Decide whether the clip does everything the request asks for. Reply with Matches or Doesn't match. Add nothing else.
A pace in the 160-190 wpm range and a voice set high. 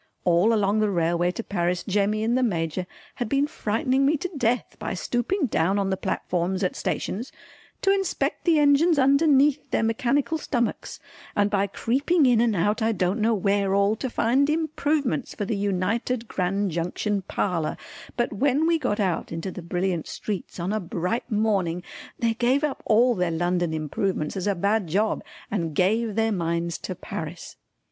Matches